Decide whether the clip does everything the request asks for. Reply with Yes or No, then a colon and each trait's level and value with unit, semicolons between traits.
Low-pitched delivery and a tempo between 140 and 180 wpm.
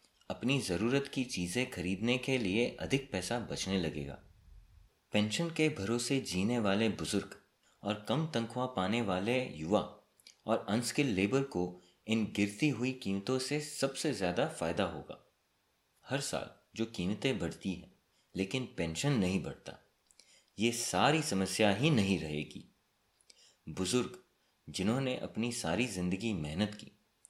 No: low, 110 Hz; average, 130 wpm